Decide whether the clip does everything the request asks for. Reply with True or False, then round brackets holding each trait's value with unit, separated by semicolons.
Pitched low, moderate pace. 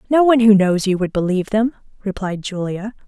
False (205 Hz; 195 wpm)